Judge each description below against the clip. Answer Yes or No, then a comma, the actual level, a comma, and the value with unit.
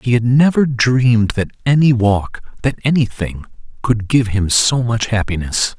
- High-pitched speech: No, low, 120 Hz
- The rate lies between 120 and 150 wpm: Yes, slow, 135 wpm